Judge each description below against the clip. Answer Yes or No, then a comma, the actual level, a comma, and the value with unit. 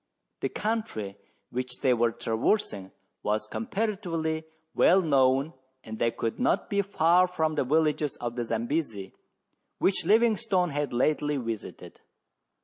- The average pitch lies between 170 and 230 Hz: No, medium, 150 Hz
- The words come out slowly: Yes, slow, 130 wpm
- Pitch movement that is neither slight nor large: No, wide, 7.4 semitones